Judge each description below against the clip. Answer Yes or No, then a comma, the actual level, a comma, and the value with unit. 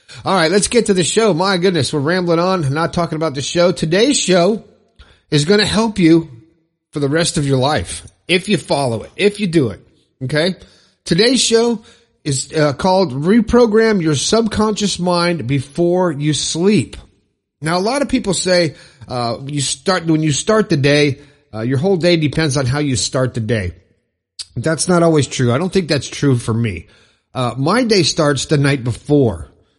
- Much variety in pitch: Yes, wide, 5.8 semitones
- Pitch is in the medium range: Yes, medium, 160 Hz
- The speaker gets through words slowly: No, average, 190 wpm